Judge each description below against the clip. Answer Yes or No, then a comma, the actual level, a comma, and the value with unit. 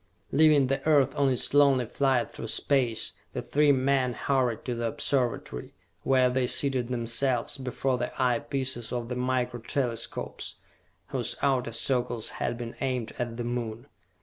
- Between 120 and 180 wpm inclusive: Yes, average, 155 wpm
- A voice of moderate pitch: No, low, 125 Hz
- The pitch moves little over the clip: Yes, narrow, 2.2 semitones